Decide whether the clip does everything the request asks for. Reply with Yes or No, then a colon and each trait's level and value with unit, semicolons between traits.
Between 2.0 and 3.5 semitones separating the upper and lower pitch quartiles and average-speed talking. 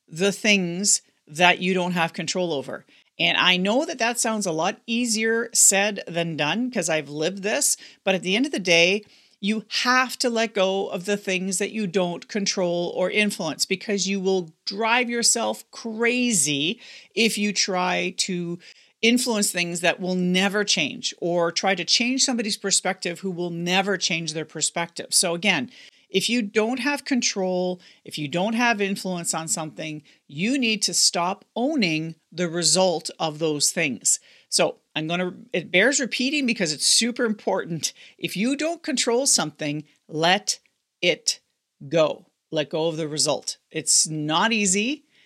No: average, 4.8 semitones; average, 165 wpm